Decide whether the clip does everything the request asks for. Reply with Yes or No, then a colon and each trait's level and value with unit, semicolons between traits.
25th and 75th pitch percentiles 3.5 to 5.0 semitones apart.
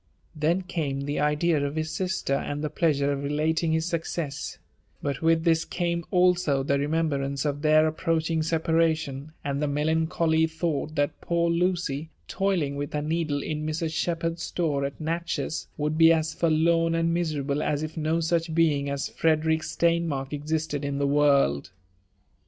No: narrow, 2.4 semitones